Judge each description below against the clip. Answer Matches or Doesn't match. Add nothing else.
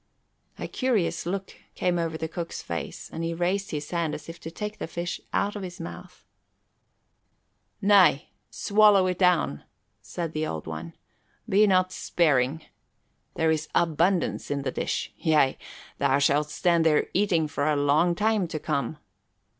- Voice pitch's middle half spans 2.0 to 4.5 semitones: Matches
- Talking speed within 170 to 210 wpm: Doesn't match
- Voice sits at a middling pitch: Matches